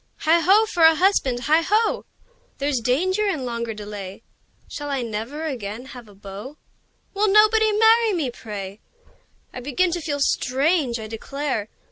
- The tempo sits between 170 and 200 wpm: No, average, 155 wpm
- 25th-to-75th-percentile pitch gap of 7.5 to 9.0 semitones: Yes, wide, 7.9 semitones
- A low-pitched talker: No, very high, 280 Hz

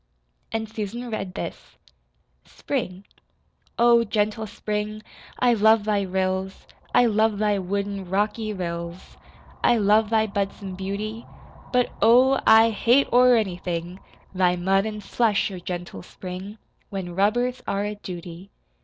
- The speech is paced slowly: Yes, slow, 130 wpm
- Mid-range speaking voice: No, high, 205 Hz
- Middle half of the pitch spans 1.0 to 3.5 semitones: Yes, average, 2.8 semitones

